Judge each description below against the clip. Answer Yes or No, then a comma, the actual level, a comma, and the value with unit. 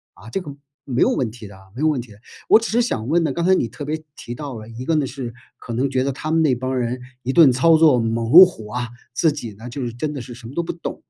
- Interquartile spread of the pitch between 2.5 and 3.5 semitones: No, average, 4.8 semitones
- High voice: No, low, 130 Hz